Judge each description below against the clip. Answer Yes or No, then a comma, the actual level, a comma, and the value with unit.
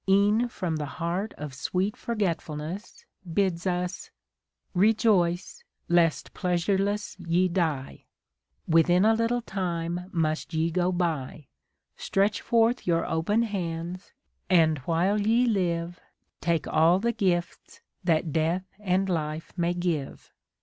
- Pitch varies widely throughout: No, average, 3.2 semitones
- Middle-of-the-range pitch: Yes, medium, 175 Hz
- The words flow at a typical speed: No, slow, 120 wpm